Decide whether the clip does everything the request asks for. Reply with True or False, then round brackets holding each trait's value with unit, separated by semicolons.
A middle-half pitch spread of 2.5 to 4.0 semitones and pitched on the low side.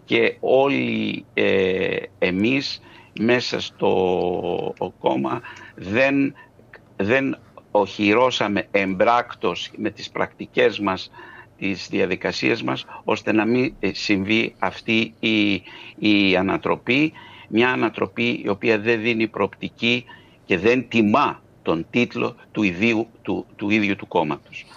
True (3.0 semitones; 115 Hz)